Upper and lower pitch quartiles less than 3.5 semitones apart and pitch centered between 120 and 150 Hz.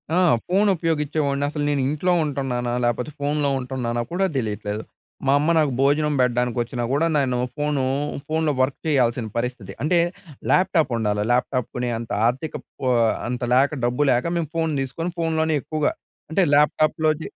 No: average, 4.0 semitones; medium, 140 Hz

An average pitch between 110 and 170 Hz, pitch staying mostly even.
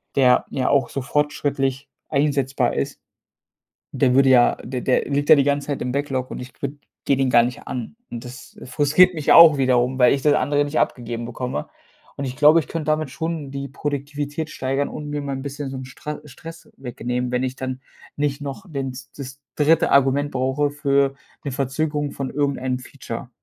Yes: medium, 140 Hz; narrow, 2.1 semitones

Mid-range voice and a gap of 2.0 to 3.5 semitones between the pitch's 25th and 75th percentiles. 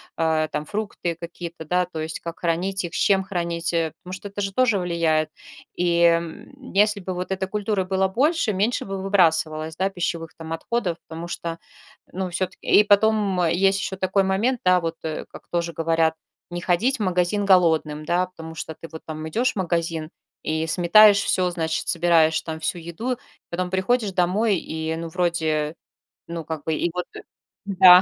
Yes: medium, 175 Hz; average, 2.9 semitones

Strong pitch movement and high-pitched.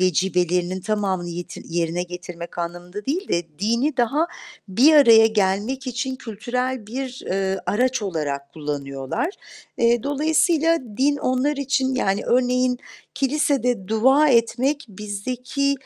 Yes: wide, 6.2 semitones; high, 230 Hz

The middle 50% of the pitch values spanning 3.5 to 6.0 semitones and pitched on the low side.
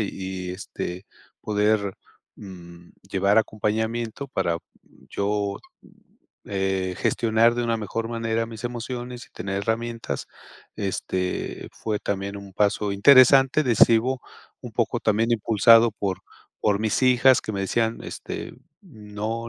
No: average, 2.7 semitones; low, 110 Hz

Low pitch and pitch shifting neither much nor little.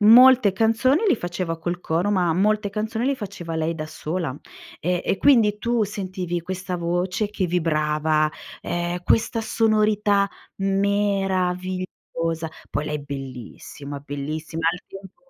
No: medium, 185 Hz; average, 4.1 semitones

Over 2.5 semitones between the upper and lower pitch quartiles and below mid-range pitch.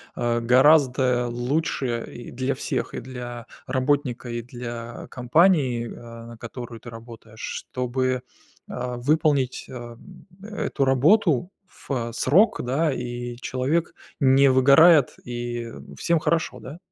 Yes: average, 2.9 semitones; low, 125 Hz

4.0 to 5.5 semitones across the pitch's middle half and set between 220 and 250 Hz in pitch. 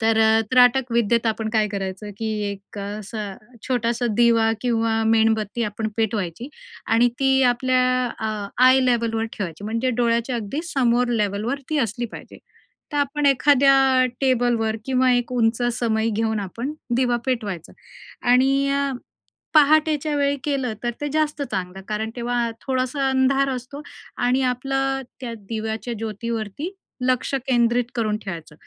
No: average, 3.0 semitones; high, 235 Hz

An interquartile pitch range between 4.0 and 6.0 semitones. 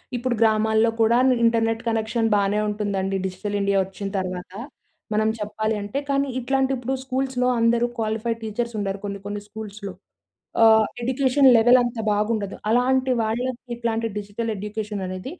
No: average, 2.8 semitones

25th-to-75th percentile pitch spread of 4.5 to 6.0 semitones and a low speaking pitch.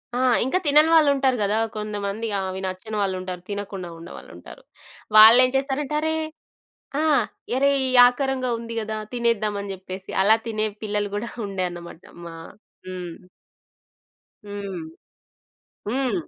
No: average, 4.8 semitones; high, 215 Hz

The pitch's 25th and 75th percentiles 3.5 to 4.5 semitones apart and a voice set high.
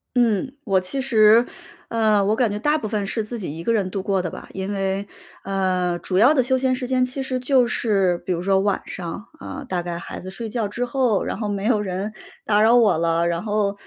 Yes: average, 4.1 semitones; high, 210 Hz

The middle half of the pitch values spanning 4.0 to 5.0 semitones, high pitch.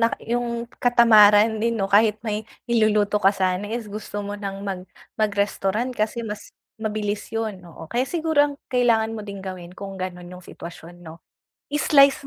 No: average, 3.0 semitones; high, 210 Hz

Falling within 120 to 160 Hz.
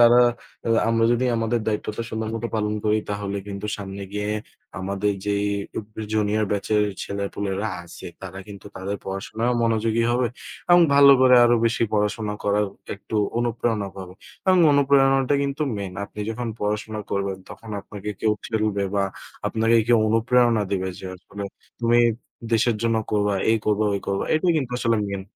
No: low, 110 Hz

